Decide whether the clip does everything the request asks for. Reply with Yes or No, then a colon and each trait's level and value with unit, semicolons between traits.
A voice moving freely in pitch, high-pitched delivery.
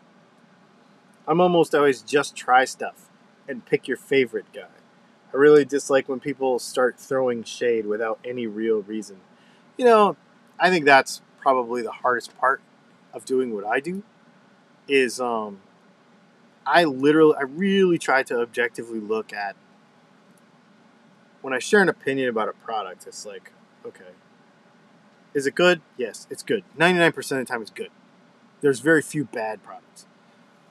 Yes: wide, 7.7 semitones; high, 200 Hz